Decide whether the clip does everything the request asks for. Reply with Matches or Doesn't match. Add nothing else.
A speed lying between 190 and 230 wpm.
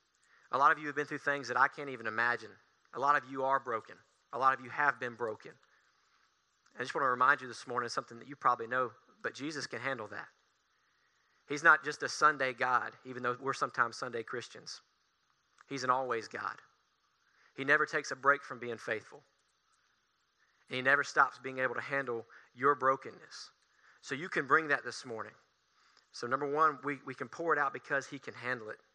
Matches